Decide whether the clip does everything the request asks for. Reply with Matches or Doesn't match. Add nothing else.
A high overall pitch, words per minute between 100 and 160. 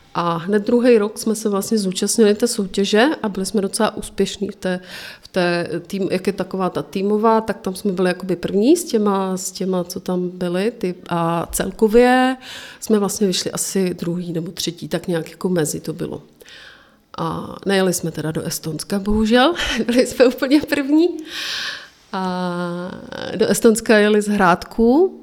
Doesn't match